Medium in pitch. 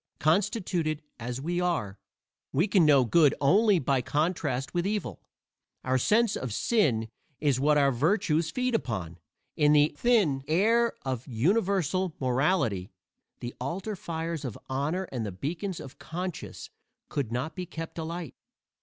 Yes: medium, 155 Hz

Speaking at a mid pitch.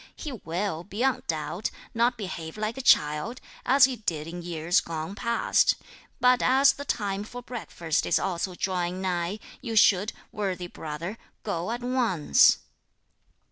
No: high, 195 Hz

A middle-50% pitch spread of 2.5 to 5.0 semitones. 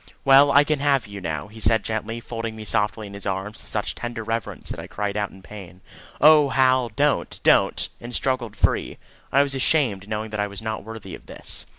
Yes: average, 4.0 semitones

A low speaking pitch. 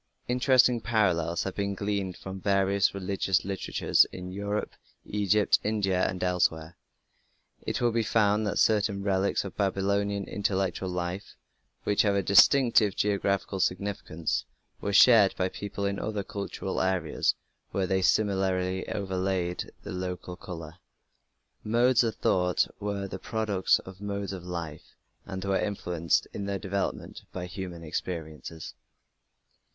Yes: very low, 95 Hz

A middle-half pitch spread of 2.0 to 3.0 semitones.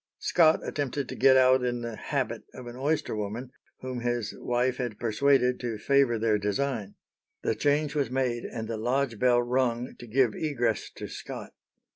Yes: narrow, 2.5 semitones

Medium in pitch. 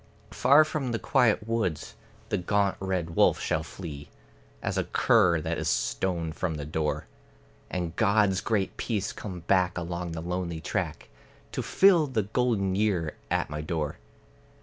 No: very low, 95 Hz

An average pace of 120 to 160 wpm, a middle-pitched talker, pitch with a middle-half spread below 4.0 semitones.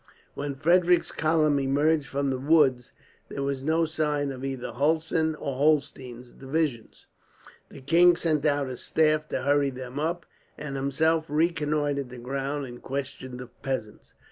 Yes: average, 150 wpm; medium, 145 Hz; average, 2.8 semitones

